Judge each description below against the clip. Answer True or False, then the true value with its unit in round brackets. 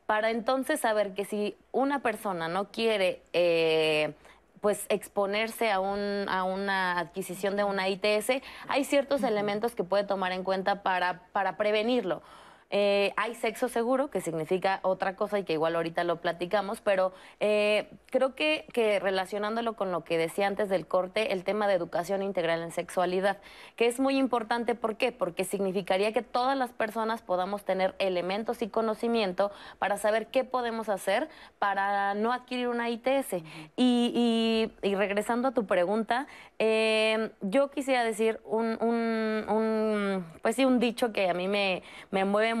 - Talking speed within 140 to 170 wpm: True (165 wpm)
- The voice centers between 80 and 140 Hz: False (205 Hz)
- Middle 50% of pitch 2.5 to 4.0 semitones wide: True (3.4 semitones)